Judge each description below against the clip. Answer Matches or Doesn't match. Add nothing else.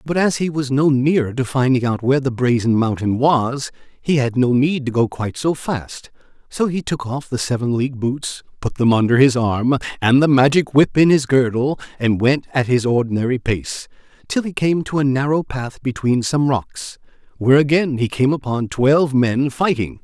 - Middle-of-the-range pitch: Doesn't match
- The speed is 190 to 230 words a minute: Matches